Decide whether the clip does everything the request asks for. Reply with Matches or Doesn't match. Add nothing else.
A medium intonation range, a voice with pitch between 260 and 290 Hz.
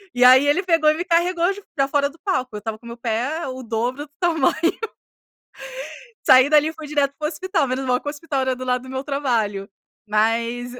Matches